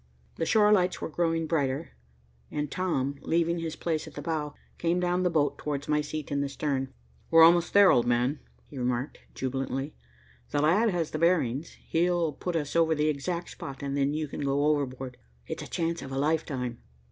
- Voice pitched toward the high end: No, medium, 150 Hz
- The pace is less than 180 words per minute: No, average, 195 wpm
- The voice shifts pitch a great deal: No, average, 3.4 semitones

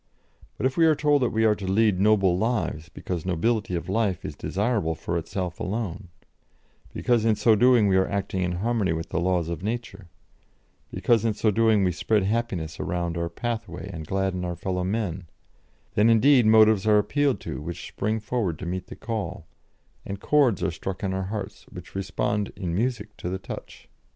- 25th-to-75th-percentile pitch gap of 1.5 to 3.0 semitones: No, average, 3.8 semitones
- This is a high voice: No, low, 100 Hz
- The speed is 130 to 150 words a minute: No, average, 190 wpm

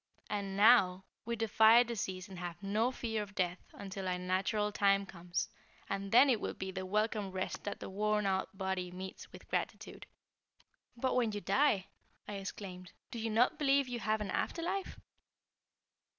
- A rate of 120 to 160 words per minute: No, average, 175 wpm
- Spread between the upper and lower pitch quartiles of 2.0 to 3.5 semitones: Yes, average, 2.9 semitones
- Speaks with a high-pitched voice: Yes, high, 200 Hz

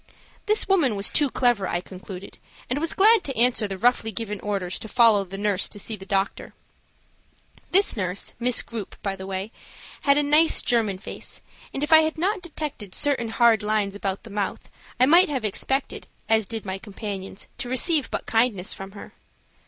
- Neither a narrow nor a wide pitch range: No, wide, 5.7 semitones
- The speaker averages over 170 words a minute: Yes, average, 190 wpm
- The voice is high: Yes, high, 220 Hz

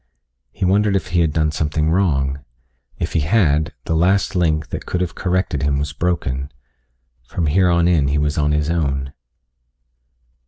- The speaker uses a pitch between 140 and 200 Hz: No, very low, 80 Hz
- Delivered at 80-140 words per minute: No, average, 170 wpm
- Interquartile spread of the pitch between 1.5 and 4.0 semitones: Yes, average, 3.4 semitones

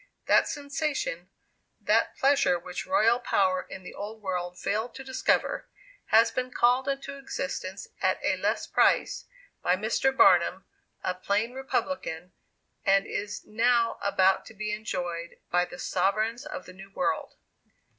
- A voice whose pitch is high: Yes, high, 215 Hz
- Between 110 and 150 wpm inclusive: Yes, average, 145 wpm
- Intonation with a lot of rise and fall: Yes, wide, 5.9 semitones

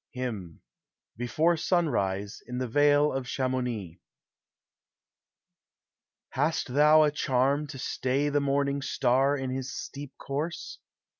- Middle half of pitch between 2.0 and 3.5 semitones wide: Yes, average, 2.7 semitones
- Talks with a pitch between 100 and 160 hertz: Yes, low, 135 Hz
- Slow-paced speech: Yes, slow, 115 wpm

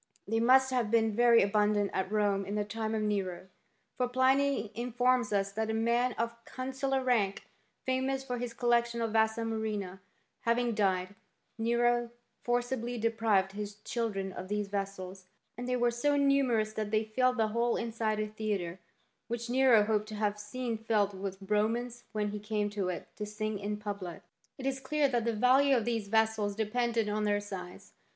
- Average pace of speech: Yes, average, 185 wpm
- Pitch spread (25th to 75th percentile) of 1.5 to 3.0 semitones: Yes, average, 2.7 semitones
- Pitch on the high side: Yes, high, 220 Hz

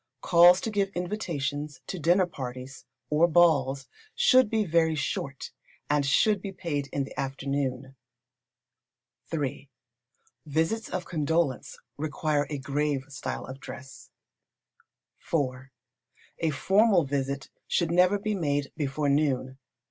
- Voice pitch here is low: No, medium, 150 Hz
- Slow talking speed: Yes, slow, 120 wpm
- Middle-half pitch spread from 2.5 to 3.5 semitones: No, average, 4.2 semitones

